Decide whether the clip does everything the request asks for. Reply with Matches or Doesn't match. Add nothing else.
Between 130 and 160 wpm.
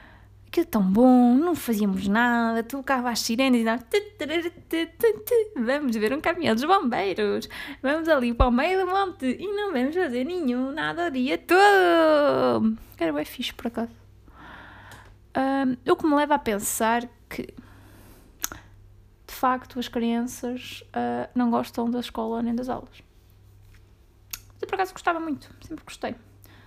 Matches